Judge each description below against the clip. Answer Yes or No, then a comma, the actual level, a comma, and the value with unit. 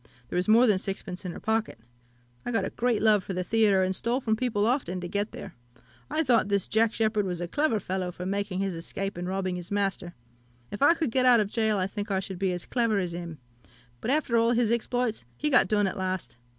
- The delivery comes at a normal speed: No, fast, 240 wpm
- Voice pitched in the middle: No, high, 205 Hz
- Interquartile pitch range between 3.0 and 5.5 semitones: Yes, average, 3.6 semitones